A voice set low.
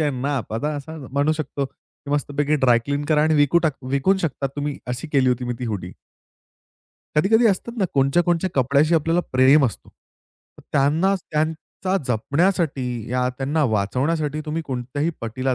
No: medium, 145 Hz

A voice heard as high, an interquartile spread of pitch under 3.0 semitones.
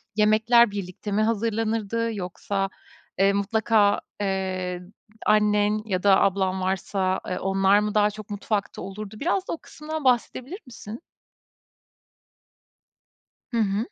Yes: high, 210 Hz; narrow, 2.4 semitones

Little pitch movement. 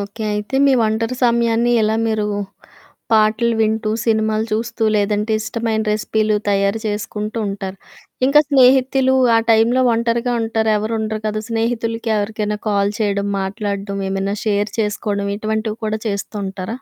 Yes: narrow, 1.7 semitones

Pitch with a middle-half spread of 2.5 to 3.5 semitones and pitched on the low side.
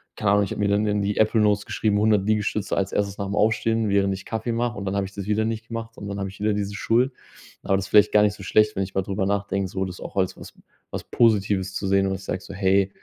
No: narrow, 1.7 semitones; low, 100 Hz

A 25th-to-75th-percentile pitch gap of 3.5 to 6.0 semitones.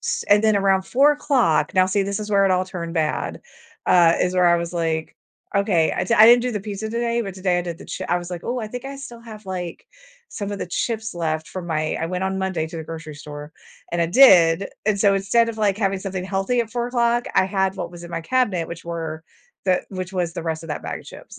Yes: average, 4.1 semitones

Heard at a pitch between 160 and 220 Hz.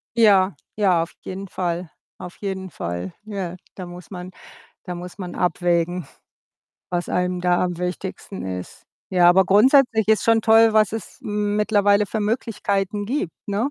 Yes: high, 190 Hz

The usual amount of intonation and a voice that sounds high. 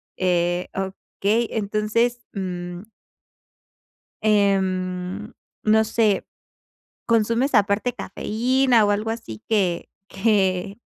Yes: average, 3.2 semitones; high, 205 Hz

